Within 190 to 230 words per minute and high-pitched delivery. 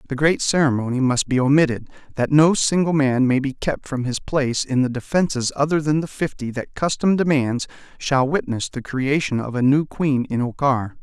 No: average, 195 wpm; medium, 140 Hz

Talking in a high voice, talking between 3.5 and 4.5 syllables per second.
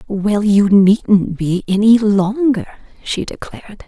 Yes: high, 205 Hz; 3.7 syllables/s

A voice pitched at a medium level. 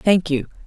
Yes: medium, 175 Hz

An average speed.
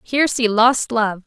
Yes: average, 190 wpm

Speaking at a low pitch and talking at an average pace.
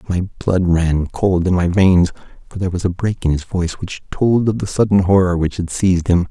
No: very low, 90 Hz; fast, 240 wpm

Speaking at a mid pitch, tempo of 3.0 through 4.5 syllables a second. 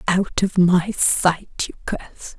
Yes: medium, 180 Hz; 4.1 syllables/s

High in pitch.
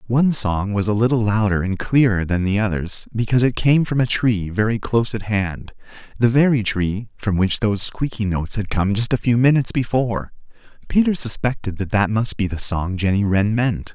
No: low, 110 Hz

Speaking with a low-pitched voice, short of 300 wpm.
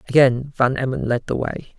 Yes: low, 130 Hz; average, 200 wpm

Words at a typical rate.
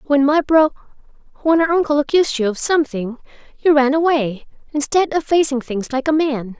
Yes: average, 165 wpm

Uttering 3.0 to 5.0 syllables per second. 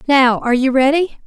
No: 5.6 syllables/s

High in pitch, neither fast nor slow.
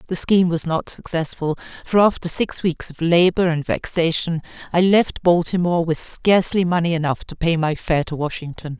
No: medium, 170 Hz; average, 175 wpm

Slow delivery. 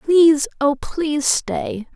Yes: slow, 125 wpm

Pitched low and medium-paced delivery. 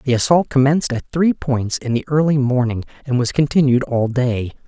Yes: low, 130 Hz; average, 190 wpm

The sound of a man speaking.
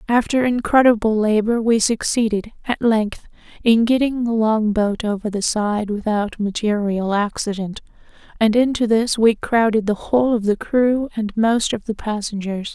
No: female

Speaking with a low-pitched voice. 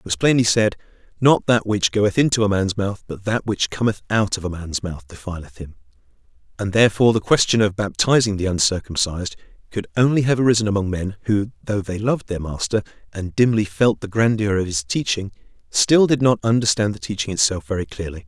Yes: low, 105 Hz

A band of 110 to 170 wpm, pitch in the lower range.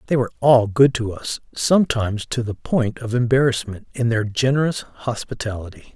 Yes: average, 160 wpm; low, 120 Hz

